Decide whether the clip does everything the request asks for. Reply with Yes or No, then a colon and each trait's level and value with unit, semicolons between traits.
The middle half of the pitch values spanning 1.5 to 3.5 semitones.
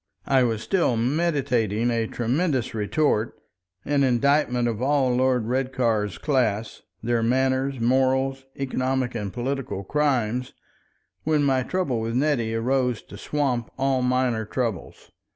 Yes: average, 2.8 semitones